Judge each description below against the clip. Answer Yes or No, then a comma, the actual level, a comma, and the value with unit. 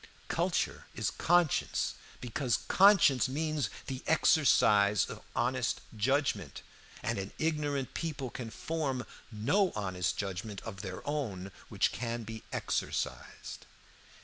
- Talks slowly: Yes, slow, 115 wpm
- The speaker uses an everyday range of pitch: No, wide, 6.1 semitones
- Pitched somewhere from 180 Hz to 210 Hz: No, low, 125 Hz